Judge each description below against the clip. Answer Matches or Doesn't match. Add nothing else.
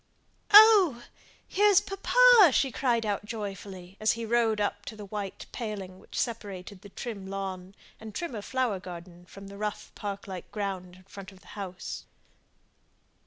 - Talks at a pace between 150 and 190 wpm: Matches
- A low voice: Doesn't match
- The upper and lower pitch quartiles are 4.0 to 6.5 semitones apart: Doesn't match